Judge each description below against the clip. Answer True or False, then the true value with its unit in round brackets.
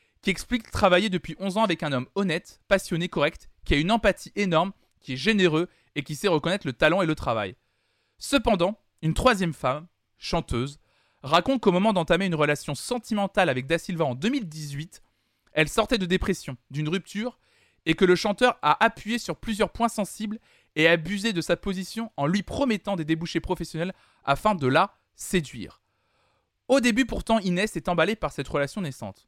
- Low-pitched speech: False (175 Hz)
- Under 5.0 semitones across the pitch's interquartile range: False (5.6 semitones)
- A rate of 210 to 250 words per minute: False (180 wpm)